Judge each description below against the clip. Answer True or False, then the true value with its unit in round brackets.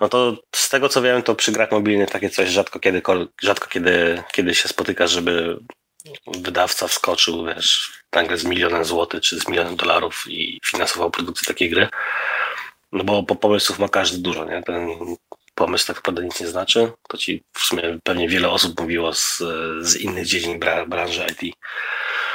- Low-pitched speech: True (90 Hz)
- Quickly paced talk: True (175 wpm)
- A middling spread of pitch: True (3.7 semitones)